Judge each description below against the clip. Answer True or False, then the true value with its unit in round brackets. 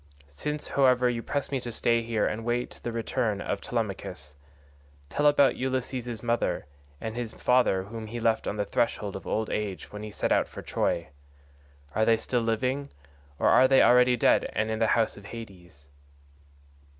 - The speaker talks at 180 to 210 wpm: True (185 wpm)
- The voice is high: False (115 Hz)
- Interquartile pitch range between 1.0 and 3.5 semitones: True (2.6 semitones)